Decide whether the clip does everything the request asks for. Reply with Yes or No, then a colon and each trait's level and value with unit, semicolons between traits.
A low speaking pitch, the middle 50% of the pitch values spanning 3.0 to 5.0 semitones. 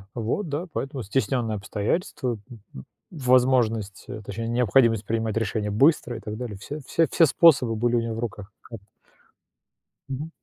Yes: low, 120 Hz; average, 3.5 semitones